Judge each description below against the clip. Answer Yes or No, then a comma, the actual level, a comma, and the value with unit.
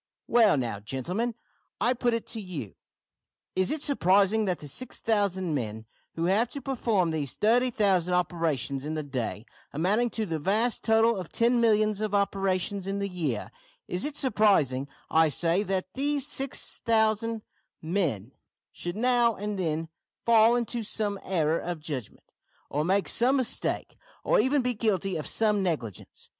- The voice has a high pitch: Yes, high, 195 Hz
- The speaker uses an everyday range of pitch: No, wide, 5.9 semitones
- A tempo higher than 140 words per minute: Yes, average, 155 wpm